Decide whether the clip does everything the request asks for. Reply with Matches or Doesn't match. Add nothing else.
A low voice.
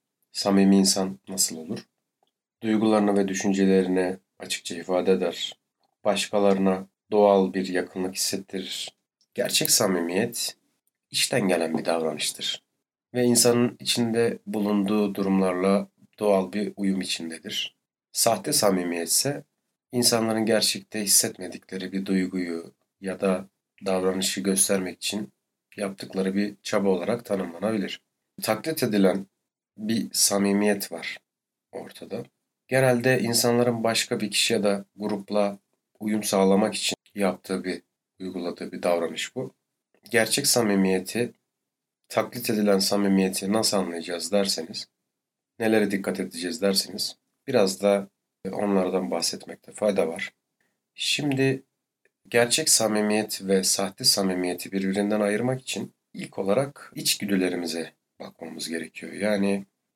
Matches